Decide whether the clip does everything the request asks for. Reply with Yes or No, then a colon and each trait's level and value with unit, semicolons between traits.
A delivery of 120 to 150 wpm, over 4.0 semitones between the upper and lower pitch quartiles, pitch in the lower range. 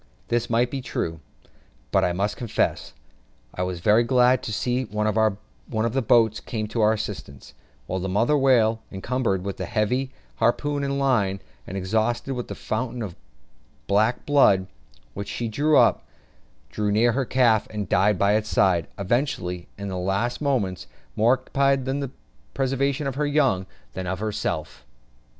No: average, 170 wpm; average, 4.6 semitones; low, 110 Hz